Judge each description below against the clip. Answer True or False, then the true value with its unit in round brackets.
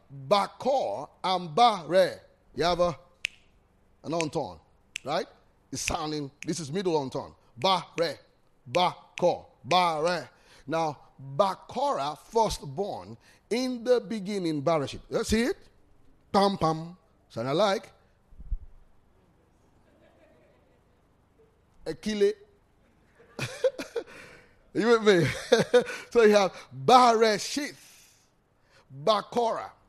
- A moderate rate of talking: False (85 wpm)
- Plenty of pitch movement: True (8.7 semitones)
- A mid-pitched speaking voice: True (180 Hz)